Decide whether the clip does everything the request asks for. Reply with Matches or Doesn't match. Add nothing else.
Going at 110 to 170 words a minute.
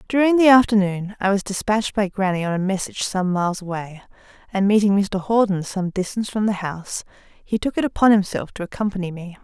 Doesn't match